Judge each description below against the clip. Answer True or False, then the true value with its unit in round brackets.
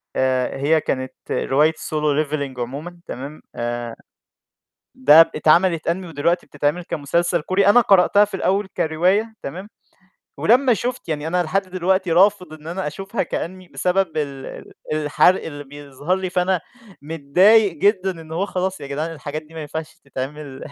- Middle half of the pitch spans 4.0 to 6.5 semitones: True (4.3 semitones)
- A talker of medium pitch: True (160 Hz)